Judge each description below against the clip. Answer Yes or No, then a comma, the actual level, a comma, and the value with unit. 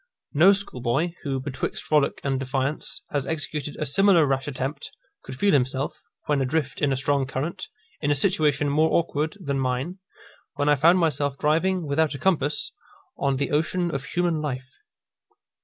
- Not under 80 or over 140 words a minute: No, average, 165 wpm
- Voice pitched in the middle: Yes, medium, 145 Hz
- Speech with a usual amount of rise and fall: Yes, average, 3.1 semitones